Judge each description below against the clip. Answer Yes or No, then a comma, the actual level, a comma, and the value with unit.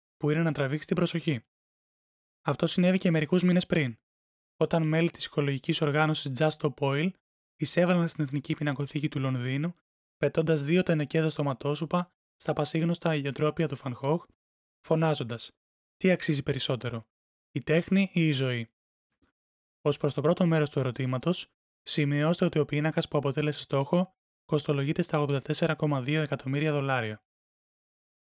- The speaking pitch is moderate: Yes, medium, 150 Hz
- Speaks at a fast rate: No, average, 135 wpm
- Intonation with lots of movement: No, average, 2.8 semitones